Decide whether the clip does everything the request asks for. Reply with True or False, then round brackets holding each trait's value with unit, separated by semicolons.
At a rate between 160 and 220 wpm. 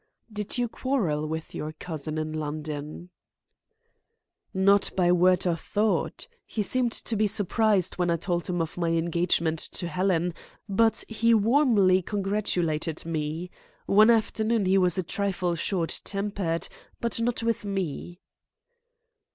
False (135 wpm)